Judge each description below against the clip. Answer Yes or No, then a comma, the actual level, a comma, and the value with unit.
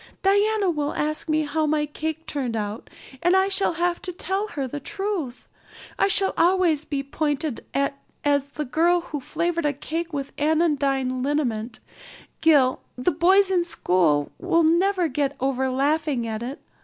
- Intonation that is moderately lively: Yes, average, 4.2 semitones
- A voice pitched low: No, very high, 305 Hz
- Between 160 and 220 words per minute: Yes, average, 165 wpm